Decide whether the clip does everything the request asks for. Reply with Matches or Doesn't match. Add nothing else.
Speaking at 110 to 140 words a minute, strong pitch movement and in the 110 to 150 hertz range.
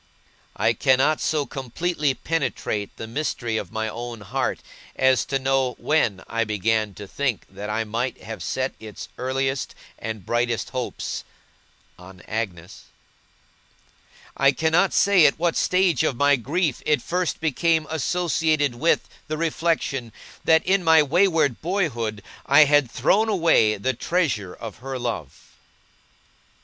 Matches